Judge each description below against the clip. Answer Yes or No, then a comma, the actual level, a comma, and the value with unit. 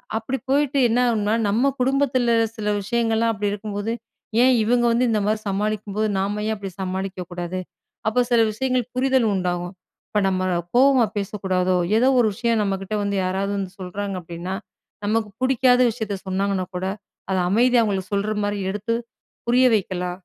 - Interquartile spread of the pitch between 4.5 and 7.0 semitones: No, average, 3.6 semitones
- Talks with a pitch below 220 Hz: Yes, high, 210 Hz